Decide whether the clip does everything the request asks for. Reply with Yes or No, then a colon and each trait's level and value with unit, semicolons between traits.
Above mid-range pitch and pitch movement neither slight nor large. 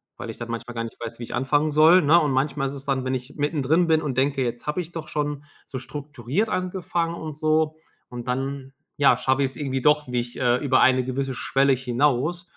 No: medium, 140 Hz; average, 3.1 semitones